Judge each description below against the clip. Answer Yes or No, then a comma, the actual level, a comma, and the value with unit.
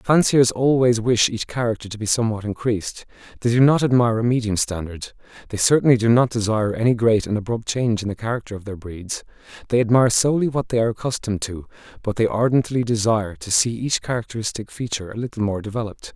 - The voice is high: No, low, 115 Hz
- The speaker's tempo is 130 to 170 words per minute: No, average, 195 wpm